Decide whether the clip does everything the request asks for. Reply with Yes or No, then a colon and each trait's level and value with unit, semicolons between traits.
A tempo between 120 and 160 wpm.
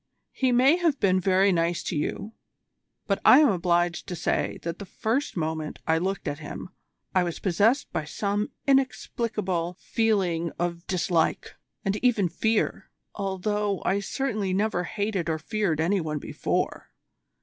Yes: average, 150 wpm